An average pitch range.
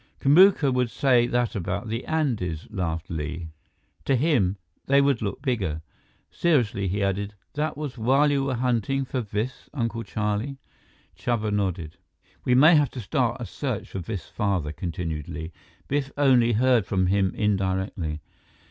No: wide, 5.8 semitones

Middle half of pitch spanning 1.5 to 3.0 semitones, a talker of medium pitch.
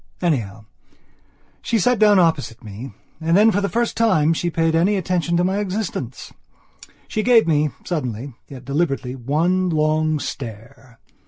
No: wide, 5.6 semitones; medium, 160 Hz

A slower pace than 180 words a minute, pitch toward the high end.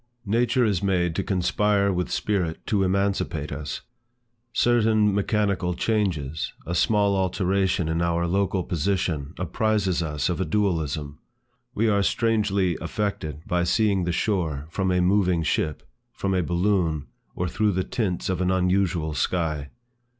No: average, 145 wpm; very low, 95 Hz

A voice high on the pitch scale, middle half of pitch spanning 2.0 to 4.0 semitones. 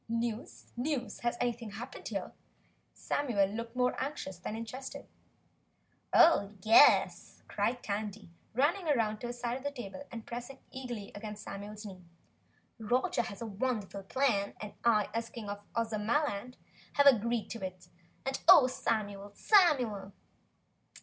Yes: high, 230 Hz; average, 3.5 semitones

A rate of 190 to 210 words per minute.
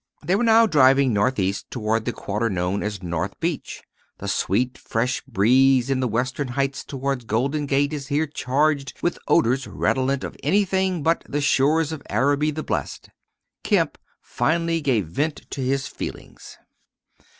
No: average, 155 wpm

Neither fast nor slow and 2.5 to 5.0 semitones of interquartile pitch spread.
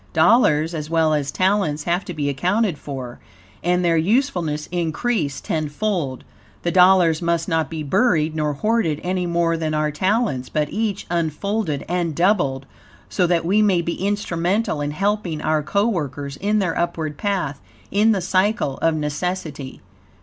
Yes: average, 155 wpm; average, 4.4 semitones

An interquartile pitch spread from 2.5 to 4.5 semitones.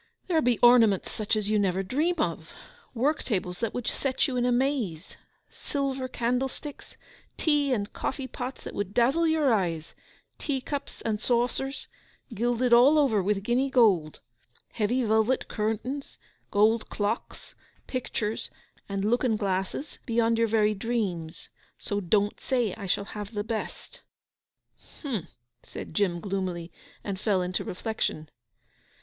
Yes: average, 4.2 semitones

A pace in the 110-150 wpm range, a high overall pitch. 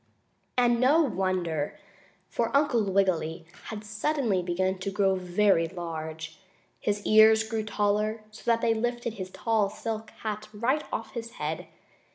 Yes: average, 145 wpm; high, 210 Hz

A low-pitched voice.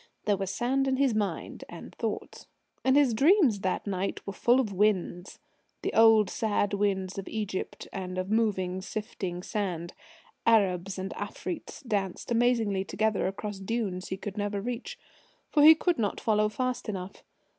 No: high, 205 Hz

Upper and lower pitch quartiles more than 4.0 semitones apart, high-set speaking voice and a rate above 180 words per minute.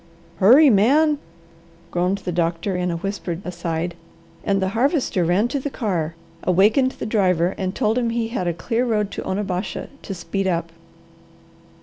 No: average, 4.4 semitones; high, 195 Hz; average, 160 wpm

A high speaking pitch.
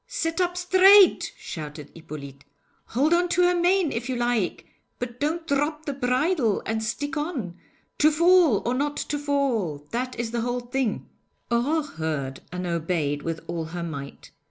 Yes: high, 245 Hz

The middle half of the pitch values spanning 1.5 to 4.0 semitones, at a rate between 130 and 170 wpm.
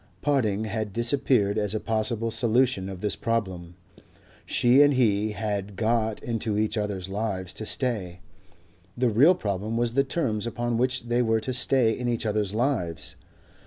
Yes: average, 2.7 semitones; average, 160 wpm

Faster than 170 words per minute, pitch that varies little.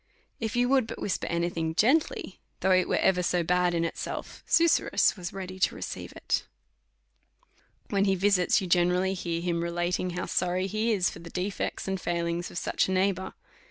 Yes: average, 195 wpm; narrow, 2.0 semitones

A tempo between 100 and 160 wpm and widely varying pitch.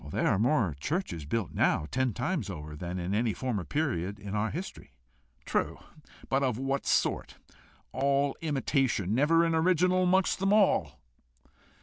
Yes: average, 150 wpm; wide, 8.6 semitones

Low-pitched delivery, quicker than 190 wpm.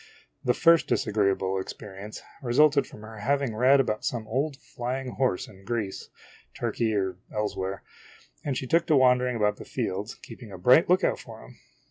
No: low, 120 Hz; average, 175 wpm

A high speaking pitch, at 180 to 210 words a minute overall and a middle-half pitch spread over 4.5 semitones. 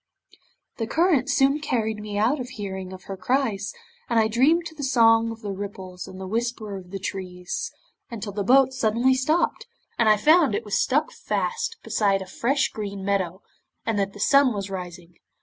Yes: high, 220 Hz; average, 190 wpm; average, 5.1 semitones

